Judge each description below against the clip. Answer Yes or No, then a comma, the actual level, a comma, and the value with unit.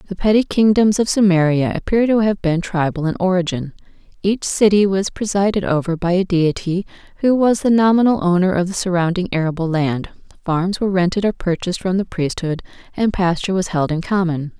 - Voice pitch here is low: No, medium, 185 Hz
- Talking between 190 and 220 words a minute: No, average, 180 wpm